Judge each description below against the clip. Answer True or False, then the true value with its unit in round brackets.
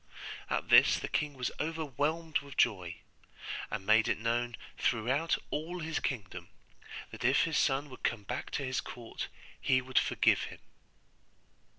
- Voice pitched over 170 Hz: False (130 Hz)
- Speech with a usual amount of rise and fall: True (4.4 semitones)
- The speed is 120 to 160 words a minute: True (155 wpm)